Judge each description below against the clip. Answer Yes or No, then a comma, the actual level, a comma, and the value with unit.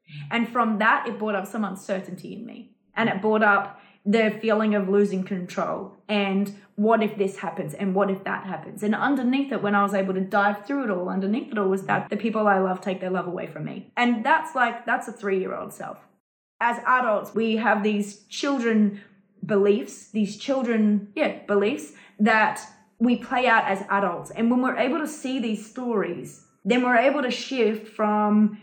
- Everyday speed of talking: Yes, average, 195 wpm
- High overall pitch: Yes, high, 210 Hz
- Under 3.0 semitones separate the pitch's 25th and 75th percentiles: Yes, narrow, 2.6 semitones